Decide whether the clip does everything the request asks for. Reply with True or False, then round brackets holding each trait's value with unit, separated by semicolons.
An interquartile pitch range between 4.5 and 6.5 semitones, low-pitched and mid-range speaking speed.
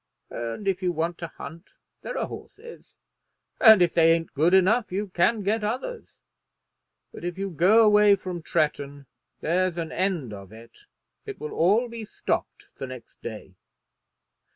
False (4.8 semitones; 180 Hz; 160 wpm)